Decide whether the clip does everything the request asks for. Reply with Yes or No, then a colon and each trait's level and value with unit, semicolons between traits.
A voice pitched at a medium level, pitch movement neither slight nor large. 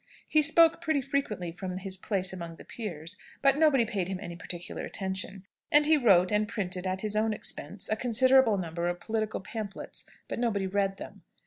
No: high, 205 Hz; average, 4.5 semitones